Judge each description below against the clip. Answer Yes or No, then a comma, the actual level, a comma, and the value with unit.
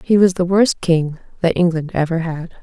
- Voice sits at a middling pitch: Yes, medium, 175 Hz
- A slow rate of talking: No, fast, 205 wpm